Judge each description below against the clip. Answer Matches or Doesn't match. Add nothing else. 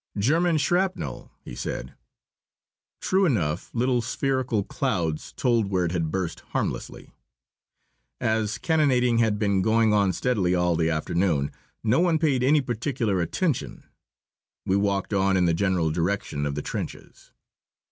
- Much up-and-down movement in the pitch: Matches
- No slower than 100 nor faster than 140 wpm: Matches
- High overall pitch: Doesn't match